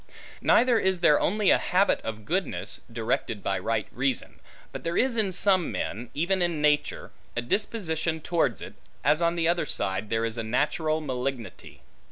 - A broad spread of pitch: Yes, wide, 7.4 semitones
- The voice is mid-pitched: Yes, medium, 155 Hz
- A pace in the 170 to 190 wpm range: Yes, average, 175 wpm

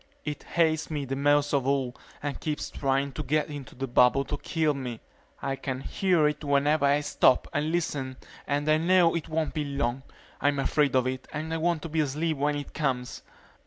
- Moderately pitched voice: Yes, medium, 145 Hz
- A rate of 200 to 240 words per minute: Yes, fast, 205 wpm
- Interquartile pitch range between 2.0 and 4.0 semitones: Yes, narrow, 2.4 semitones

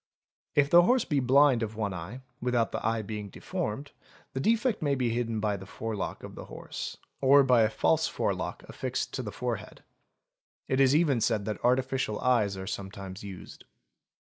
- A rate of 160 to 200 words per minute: Yes, average, 185 wpm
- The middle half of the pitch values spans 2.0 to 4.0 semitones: No, average, 4.4 semitones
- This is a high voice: No, low, 115 Hz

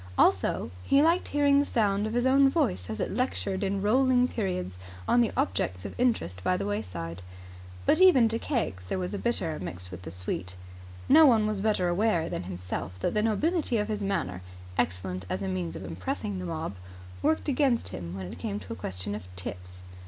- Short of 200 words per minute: No, fast, 205 wpm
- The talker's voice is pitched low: No, medium, 180 Hz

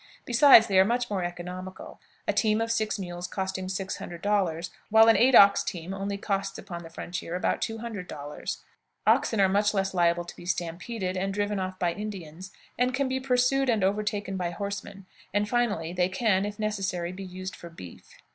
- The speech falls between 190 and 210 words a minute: Yes, average, 195 wpm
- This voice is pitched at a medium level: No, high, 195 Hz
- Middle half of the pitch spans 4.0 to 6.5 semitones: No, average, 2.9 semitones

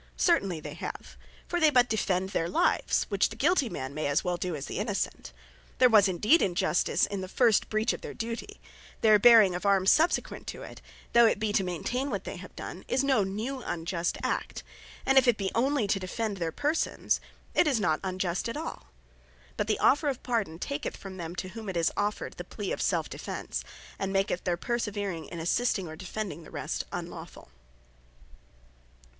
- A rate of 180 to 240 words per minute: Yes, average, 195 wpm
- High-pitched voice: Yes, high, 205 Hz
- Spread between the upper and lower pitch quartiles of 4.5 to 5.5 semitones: Yes, average, 5.0 semitones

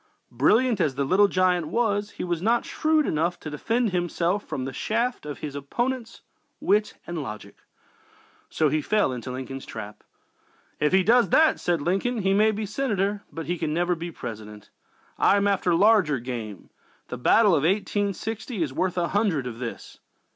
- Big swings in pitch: Yes, wide, 6.2 semitones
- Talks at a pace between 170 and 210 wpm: Yes, average, 175 wpm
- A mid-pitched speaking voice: Yes, medium, 180 Hz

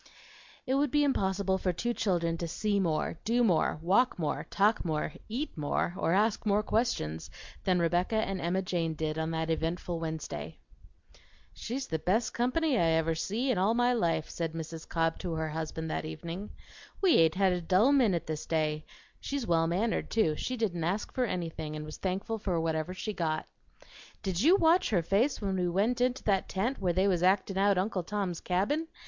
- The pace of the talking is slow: No, average, 195 wpm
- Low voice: No, medium, 185 Hz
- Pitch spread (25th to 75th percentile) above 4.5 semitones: Yes, average, 5.1 semitones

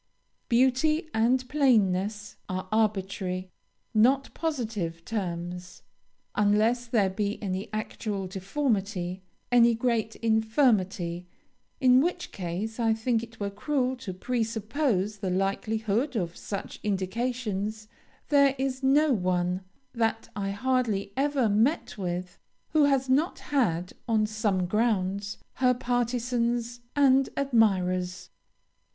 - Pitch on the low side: No, high, 220 Hz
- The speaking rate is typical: No, slow, 110 wpm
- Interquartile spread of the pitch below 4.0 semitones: No, average, 4.6 semitones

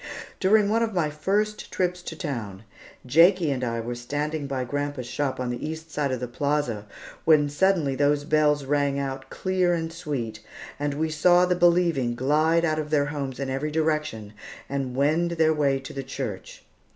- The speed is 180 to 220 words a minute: Yes, average, 185 wpm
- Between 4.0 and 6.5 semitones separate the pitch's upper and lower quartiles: No, average, 3.4 semitones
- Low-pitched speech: No, medium, 145 Hz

